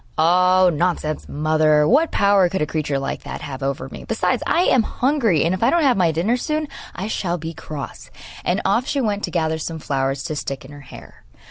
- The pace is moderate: No, fast, 220 wpm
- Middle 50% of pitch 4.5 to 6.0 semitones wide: Yes, average, 5.3 semitones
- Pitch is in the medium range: Yes, medium, 170 Hz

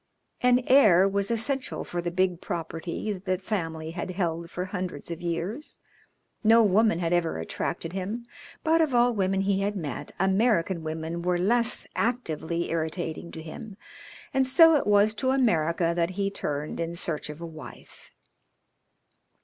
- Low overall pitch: No, medium, 185 Hz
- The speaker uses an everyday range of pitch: Yes, average, 4.6 semitones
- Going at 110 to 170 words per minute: Yes, average, 160 wpm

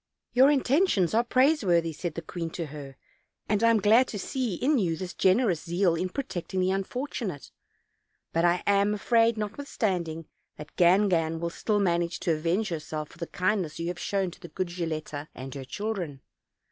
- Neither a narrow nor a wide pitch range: Yes, average, 4.5 semitones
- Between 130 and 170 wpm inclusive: No, average, 185 wpm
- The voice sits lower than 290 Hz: Yes, medium, 185 Hz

